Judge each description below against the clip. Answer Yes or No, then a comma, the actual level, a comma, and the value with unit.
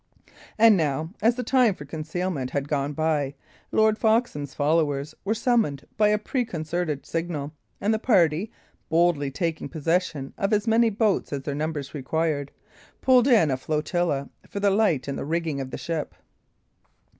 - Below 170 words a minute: Yes, average, 160 wpm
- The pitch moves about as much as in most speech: No, wide, 6.5 semitones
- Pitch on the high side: No, medium, 165 Hz